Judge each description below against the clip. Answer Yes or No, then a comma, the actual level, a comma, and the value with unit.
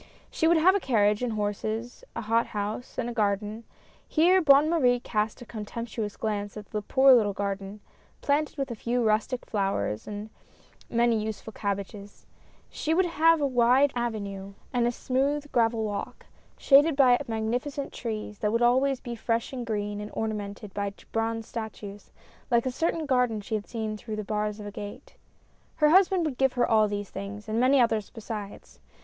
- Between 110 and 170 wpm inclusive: No, average, 185 wpm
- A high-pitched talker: Yes, high, 225 Hz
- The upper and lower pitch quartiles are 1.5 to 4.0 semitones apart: Yes, average, 3.6 semitones